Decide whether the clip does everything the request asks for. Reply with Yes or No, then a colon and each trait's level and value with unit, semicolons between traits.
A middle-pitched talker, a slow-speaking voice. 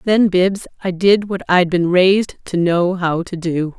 No: medium, 180 Hz; fast, 205 wpm